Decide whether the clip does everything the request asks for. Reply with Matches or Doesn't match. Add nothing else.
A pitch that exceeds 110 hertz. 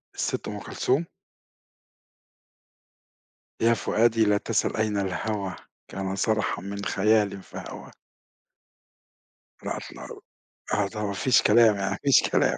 Doesn't match